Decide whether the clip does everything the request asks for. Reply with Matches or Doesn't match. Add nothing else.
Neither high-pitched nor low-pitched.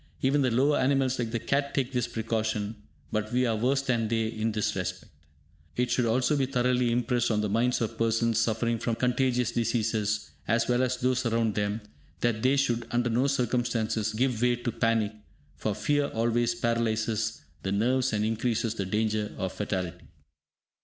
Doesn't match